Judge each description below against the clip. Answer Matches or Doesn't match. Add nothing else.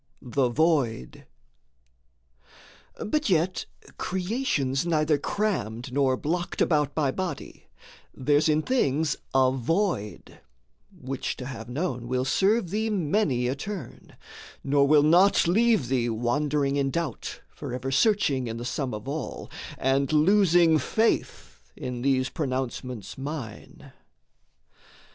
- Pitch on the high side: Doesn't match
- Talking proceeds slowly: Matches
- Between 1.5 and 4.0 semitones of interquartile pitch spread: Doesn't match